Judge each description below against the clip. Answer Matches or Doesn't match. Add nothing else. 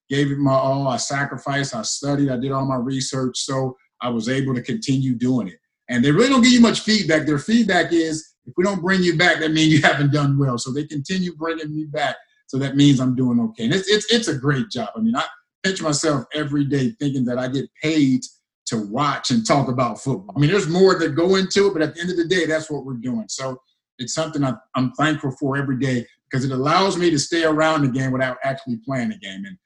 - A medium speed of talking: Doesn't match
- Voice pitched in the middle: Matches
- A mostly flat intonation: Doesn't match